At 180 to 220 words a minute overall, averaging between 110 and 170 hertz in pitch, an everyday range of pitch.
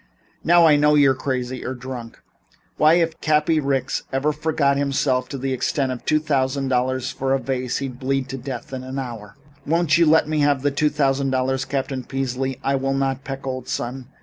No: average, 200 wpm; low, 135 Hz; narrow, 1.9 semitones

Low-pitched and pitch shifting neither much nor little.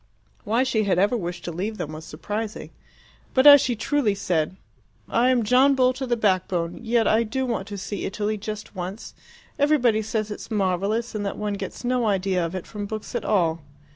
No: high, 215 Hz; average, 4.0 semitones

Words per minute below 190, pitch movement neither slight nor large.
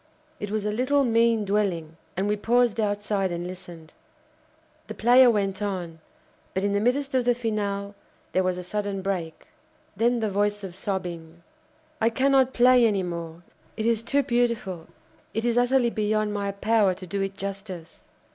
Yes: average, 170 wpm; average, 3.7 semitones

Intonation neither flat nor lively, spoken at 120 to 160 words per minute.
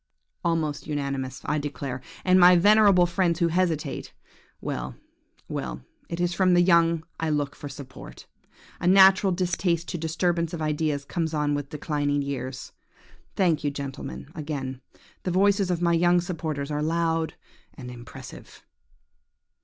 Yes: average, 3.5 semitones; slow, 135 wpm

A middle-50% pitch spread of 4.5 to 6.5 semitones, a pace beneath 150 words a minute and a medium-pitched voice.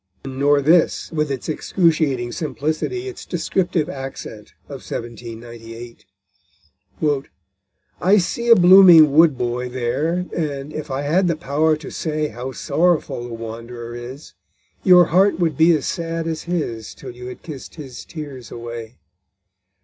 Yes: wide, 5.5 semitones; average, 140 wpm; medium, 145 Hz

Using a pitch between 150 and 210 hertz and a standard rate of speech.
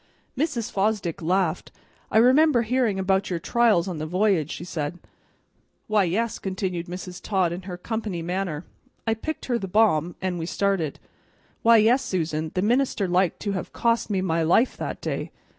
Yes: high, 190 Hz; average, 175 wpm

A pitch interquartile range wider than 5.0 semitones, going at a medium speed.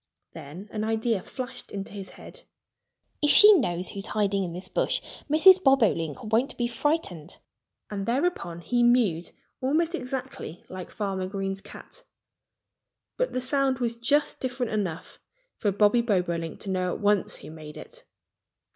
Yes: wide, 5.6 semitones; average, 150 wpm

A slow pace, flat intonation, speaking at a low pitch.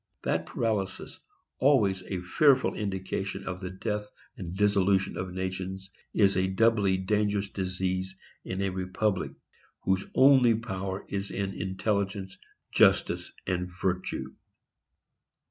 Yes: slow, 115 wpm; narrow, 1.7 semitones; very low, 95 Hz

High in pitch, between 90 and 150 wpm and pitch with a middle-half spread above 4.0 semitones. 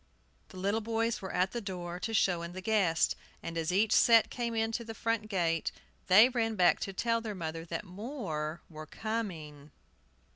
No: high, 195 Hz; average, 185 wpm; average, 4.9 semitones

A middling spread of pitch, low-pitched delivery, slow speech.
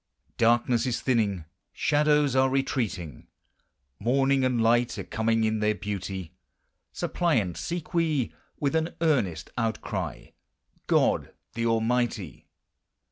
Yes: average, 4.2 semitones; low, 120 Hz; slow, 110 wpm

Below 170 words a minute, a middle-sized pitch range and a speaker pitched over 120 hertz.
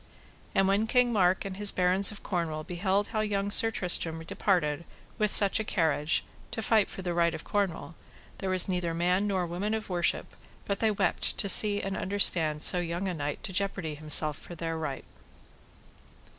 No: average, 185 wpm; average, 3.3 semitones; medium, 185 Hz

